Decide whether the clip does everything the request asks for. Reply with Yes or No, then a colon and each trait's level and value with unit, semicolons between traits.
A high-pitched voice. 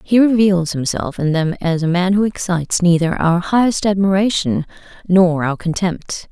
No: medium, 180 Hz